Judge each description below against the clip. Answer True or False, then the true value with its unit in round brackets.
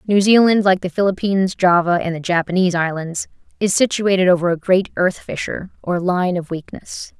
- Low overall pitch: False (185 Hz)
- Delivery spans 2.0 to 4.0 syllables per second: False (5.5 syllables/s)